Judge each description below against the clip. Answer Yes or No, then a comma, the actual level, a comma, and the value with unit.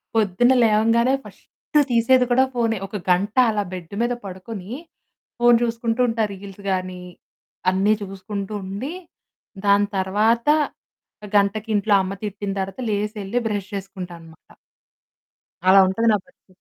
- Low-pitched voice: No, high, 205 Hz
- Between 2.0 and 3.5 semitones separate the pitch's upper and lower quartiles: Yes, average, 3.1 semitones